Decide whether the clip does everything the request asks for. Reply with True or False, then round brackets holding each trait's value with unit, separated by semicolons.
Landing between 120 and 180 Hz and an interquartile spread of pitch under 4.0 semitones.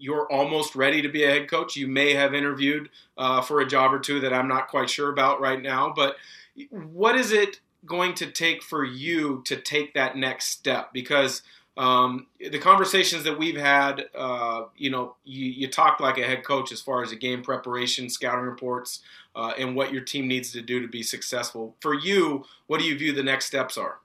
True (135 Hz; 2.6 semitones)